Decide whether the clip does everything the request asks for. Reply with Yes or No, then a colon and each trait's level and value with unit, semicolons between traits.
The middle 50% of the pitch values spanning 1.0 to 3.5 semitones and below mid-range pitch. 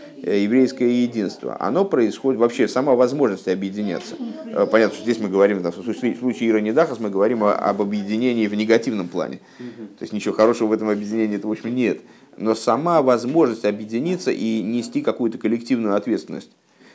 Yes: narrow, 2.5 semitones; low, 110 Hz